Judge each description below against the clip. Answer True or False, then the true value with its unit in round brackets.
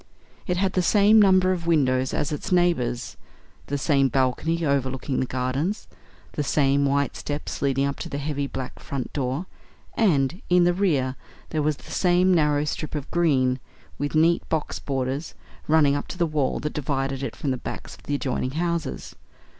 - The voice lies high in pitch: False (145 Hz)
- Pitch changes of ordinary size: True (4.0 semitones)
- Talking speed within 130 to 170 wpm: False (180 wpm)